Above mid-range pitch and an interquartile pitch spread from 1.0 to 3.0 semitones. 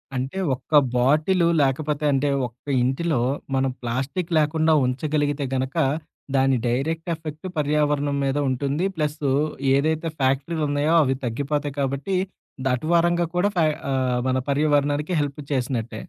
No: medium, 145 Hz; average, 2.7 semitones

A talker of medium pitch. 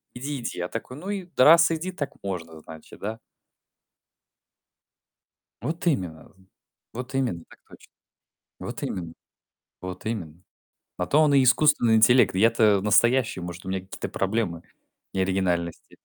No: low, 110 Hz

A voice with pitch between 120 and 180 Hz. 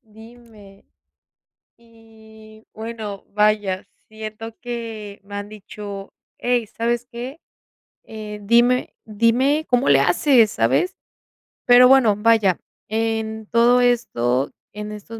No: high, 220 Hz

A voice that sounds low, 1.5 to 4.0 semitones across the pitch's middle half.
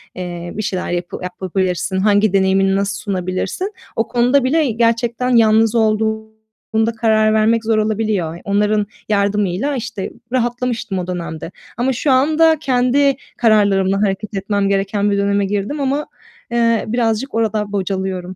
No: high, 215 Hz; average, 3.3 semitones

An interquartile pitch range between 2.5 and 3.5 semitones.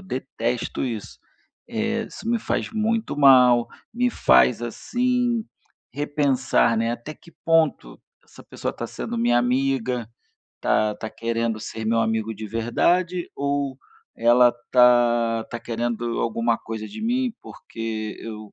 No: average, 4.8 semitones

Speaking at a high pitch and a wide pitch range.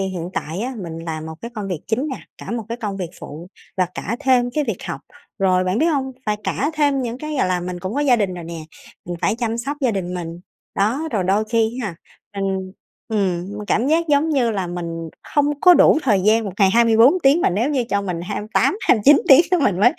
Yes: high, 215 Hz; wide, 6.2 semitones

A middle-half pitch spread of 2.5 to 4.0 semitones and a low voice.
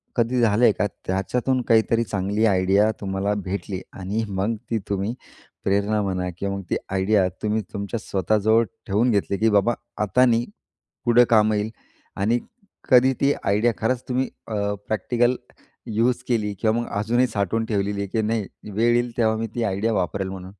Yes: average, 2.8 semitones; low, 110 Hz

